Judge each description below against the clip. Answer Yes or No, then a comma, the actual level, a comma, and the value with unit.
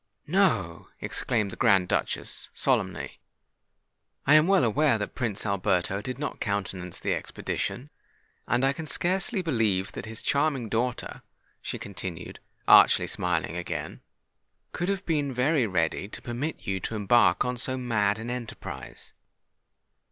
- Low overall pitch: Yes, low, 120 Hz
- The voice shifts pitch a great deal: Yes, wide, 6.2 semitones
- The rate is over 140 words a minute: No, slow, 135 wpm